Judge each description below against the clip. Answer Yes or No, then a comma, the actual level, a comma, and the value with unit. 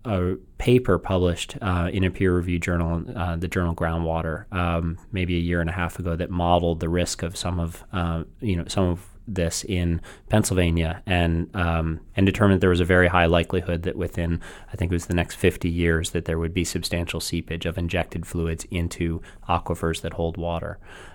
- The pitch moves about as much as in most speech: No, narrow, 1.6 semitones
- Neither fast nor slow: Yes, average, 195 wpm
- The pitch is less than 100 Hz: Yes, very low, 85 Hz